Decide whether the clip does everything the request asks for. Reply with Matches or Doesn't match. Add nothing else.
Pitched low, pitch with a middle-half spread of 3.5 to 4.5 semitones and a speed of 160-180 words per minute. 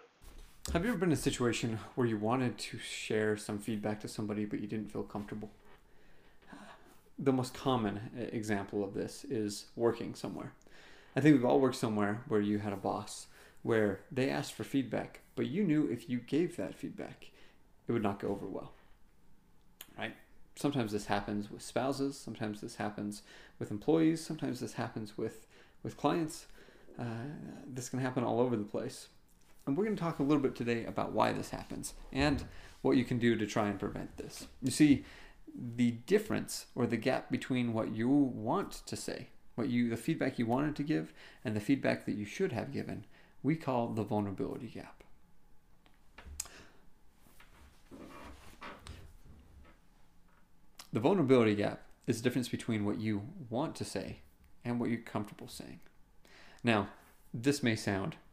Matches